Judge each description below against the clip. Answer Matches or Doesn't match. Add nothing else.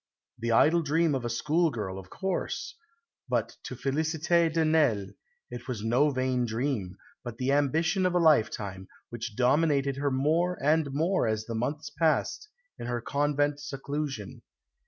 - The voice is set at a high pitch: Doesn't match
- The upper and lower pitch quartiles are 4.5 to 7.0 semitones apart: Matches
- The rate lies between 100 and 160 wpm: Matches